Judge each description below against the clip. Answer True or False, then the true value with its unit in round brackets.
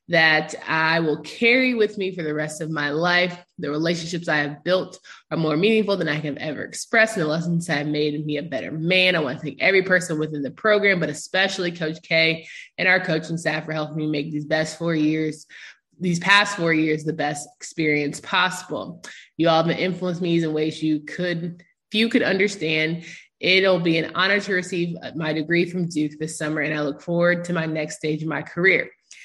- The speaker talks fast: True (210 wpm)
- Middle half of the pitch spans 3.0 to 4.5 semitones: False (2.6 semitones)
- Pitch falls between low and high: True (160 Hz)